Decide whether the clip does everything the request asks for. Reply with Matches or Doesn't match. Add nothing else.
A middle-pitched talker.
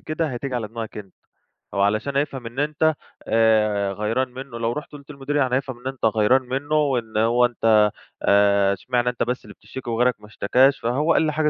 Doesn't match